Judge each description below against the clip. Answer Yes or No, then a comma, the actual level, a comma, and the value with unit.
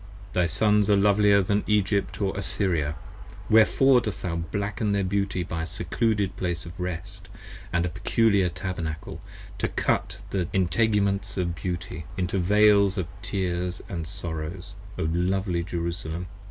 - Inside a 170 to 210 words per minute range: No, average, 140 wpm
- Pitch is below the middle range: Yes, very low, 95 Hz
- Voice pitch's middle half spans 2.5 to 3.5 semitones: Yes, average, 2.8 semitones